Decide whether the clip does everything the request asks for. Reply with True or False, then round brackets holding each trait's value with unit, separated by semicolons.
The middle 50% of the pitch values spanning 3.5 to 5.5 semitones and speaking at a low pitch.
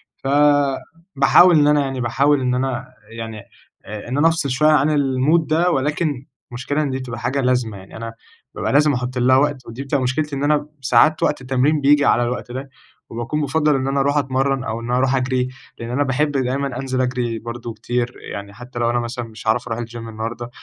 False (3.0 semitones; 130 Hz)